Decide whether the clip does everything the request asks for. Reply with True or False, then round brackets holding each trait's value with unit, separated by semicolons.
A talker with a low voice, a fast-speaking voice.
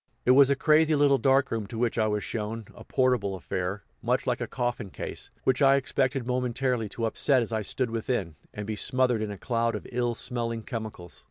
True (120 Hz; 210 wpm)